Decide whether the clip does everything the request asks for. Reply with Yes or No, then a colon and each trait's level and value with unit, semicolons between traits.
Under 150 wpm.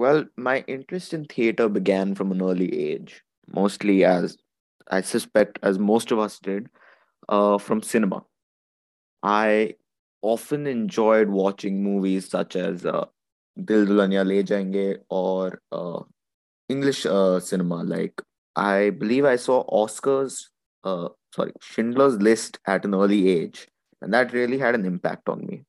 Yes: average, 140 wpm